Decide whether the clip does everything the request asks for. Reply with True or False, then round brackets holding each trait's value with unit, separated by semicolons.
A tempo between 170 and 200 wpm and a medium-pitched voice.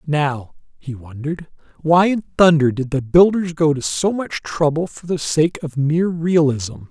True (175 wpm; 155 Hz)